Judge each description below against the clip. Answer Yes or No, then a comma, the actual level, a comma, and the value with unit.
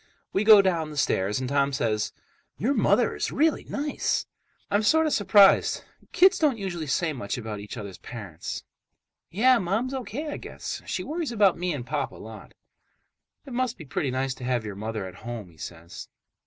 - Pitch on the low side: No, medium, 160 Hz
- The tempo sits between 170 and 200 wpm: Yes, average, 185 wpm